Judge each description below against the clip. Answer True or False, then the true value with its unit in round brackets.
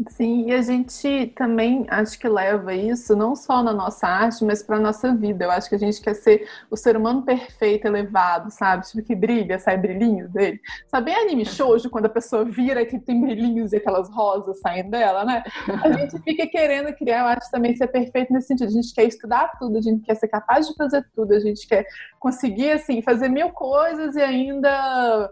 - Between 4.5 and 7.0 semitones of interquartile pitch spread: False (3.2 semitones)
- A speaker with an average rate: False (210 wpm)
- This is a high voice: True (235 Hz)